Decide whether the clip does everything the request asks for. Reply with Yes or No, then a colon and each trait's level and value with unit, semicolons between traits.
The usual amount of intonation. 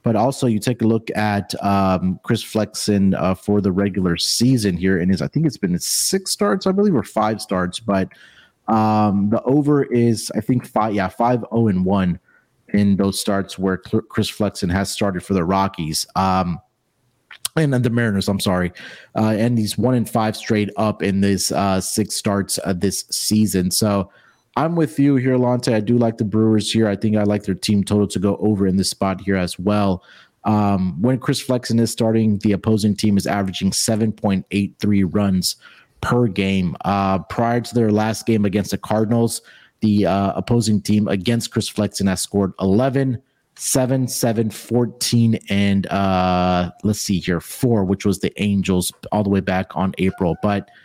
Yes: average, 3.0 semitones